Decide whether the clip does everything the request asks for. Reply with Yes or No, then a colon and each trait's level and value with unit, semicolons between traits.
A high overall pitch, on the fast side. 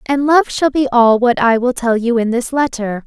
Yes: high, 245 Hz; fast, 255 wpm